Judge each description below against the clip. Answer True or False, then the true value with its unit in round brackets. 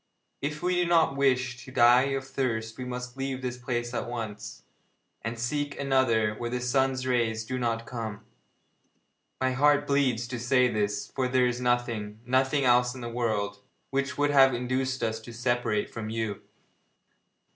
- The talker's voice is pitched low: True (125 Hz)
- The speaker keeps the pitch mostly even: True (2.3 semitones)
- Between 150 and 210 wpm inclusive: True (170 wpm)